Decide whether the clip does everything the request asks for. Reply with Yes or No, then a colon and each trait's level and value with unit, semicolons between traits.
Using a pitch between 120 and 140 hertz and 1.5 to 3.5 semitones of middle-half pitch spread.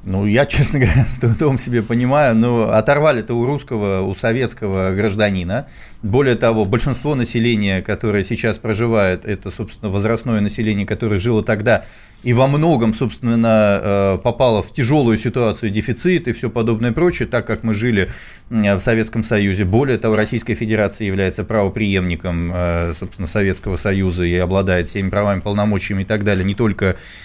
No: low, 110 Hz; average, 3.0 semitones